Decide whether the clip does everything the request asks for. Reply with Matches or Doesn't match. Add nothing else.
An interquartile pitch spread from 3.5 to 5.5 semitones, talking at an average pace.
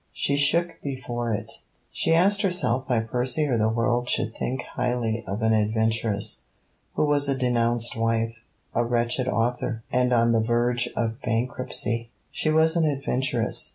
Doesn't match